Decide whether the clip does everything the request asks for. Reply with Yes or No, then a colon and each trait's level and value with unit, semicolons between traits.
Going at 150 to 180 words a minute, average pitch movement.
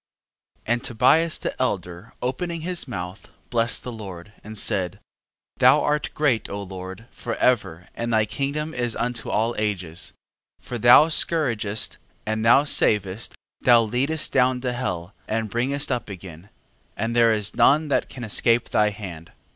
Yes: average, 160 wpm; average, 4.0 semitones